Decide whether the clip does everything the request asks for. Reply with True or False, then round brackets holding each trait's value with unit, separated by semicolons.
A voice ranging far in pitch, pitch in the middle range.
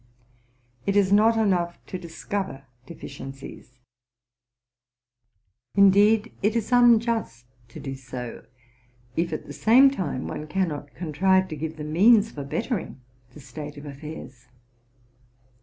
True (6.3 semitones; 170 Hz)